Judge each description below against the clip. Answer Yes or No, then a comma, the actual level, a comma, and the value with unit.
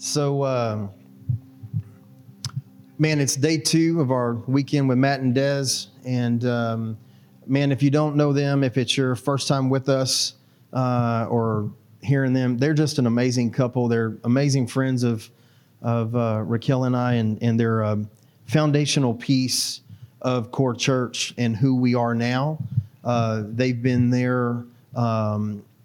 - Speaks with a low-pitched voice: Yes, low, 125 Hz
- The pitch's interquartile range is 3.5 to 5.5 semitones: No, narrow, 2.5 semitones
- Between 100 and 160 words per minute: Yes, average, 150 wpm